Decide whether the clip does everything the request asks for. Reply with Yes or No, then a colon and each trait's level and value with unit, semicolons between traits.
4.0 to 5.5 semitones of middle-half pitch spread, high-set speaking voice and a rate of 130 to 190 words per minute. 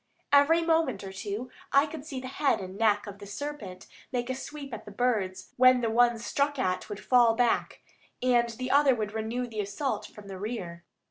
No: average, 4.4 semitones; high, 240 Hz; fast, 205 wpm